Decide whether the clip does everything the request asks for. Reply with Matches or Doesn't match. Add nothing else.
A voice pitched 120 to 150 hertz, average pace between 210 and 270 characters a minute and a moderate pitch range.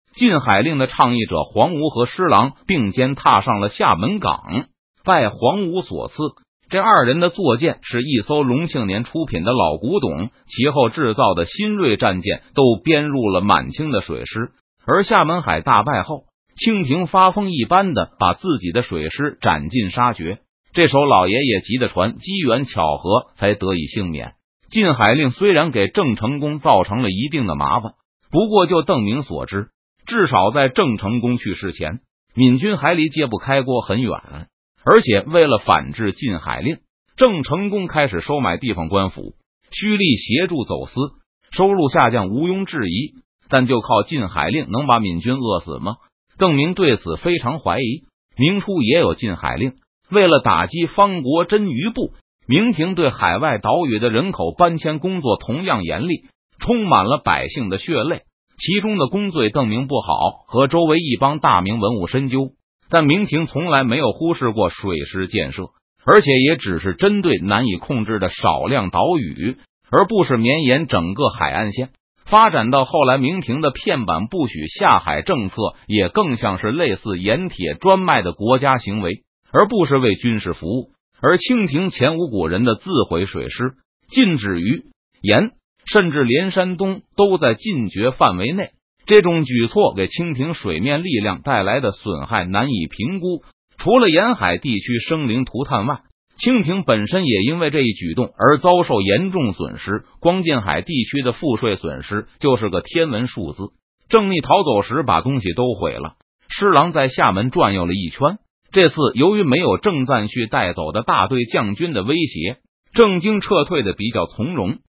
Doesn't match